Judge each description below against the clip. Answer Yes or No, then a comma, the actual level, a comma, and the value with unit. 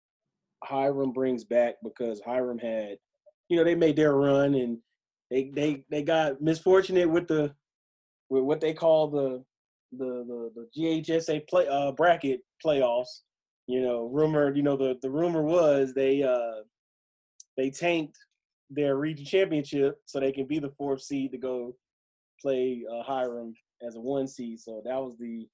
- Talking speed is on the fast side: No, average, 160 wpm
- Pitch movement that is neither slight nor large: Yes, average, 3.8 semitones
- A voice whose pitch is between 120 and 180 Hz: Yes, low, 135 Hz